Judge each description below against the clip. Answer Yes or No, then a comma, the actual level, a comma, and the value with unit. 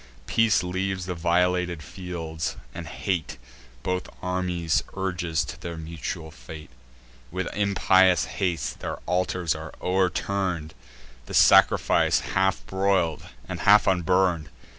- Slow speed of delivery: Yes, slow, 115 wpm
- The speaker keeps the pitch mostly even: Yes, narrow, 2.2 semitones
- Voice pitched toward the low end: Yes, very low, 90 Hz